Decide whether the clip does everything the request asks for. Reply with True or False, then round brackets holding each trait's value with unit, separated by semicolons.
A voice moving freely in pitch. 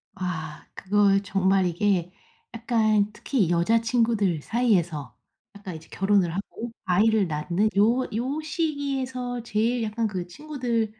False (4.5 semitones)